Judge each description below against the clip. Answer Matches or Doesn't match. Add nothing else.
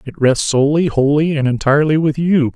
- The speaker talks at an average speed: Matches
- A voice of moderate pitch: Matches